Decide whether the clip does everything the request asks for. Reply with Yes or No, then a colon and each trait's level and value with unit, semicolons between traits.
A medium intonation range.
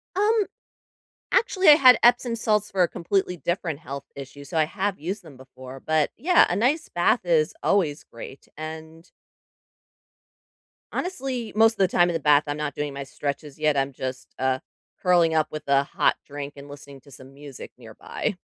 No: wide, 6.8 semitones